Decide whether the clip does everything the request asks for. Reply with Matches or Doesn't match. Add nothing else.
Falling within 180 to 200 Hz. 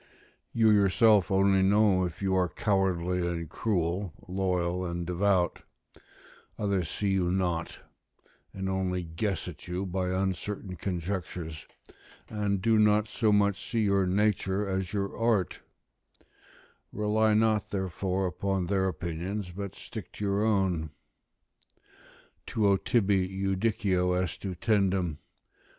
Doesn't match